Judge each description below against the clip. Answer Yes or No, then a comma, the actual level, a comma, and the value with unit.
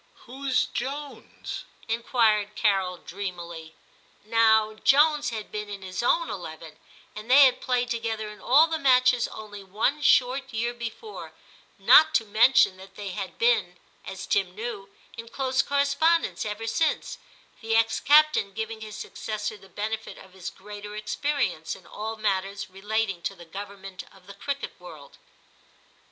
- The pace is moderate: Yes, average, 155 wpm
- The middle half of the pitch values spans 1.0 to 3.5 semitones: No, average, 4.2 semitones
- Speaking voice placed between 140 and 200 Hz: No, high, 220 Hz